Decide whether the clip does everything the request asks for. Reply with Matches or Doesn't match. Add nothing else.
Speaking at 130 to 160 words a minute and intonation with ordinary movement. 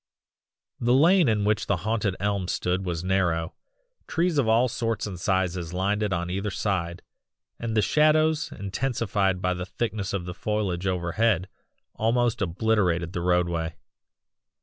Matches